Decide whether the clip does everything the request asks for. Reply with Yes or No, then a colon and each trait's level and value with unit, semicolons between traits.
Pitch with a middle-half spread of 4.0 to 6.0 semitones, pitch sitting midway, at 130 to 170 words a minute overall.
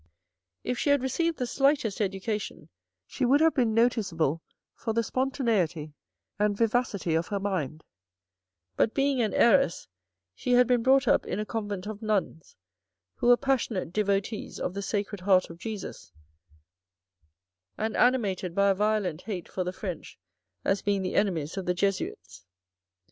No: average, 4.6 semitones; high, 205 Hz; average, 155 wpm